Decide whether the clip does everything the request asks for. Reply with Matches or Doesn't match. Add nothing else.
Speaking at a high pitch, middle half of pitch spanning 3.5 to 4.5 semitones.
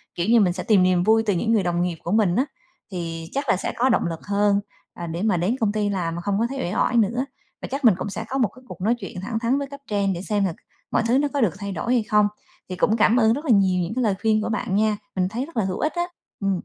Matches